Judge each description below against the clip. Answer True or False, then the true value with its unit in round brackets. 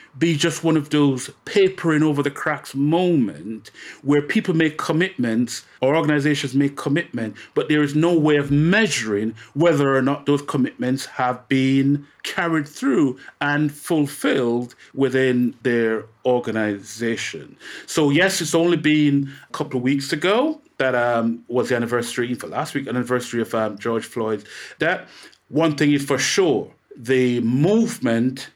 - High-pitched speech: False (140 Hz)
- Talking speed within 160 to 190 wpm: False (145 wpm)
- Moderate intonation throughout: True (4.2 semitones)